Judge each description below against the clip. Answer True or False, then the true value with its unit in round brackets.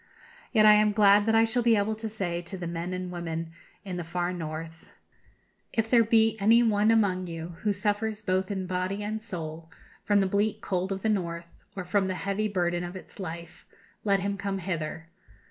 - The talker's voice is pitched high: True (195 Hz)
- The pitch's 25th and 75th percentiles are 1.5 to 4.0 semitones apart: True (3.4 semitones)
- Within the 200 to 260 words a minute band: True (205 wpm)